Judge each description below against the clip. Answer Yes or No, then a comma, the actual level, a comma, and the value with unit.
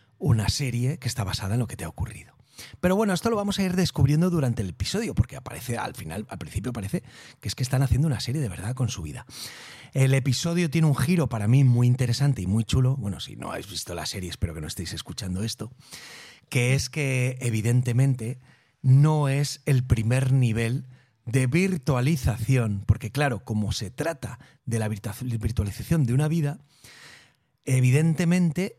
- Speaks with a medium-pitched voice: No, low, 125 Hz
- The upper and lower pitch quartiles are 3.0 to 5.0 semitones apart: Yes, average, 4.2 semitones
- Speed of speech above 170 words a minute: Yes, average, 185 wpm